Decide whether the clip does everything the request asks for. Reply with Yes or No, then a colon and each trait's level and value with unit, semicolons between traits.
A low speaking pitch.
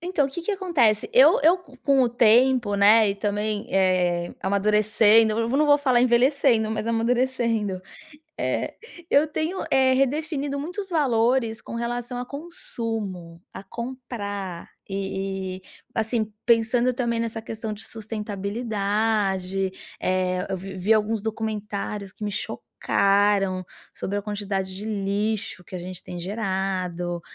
No: high, 220 Hz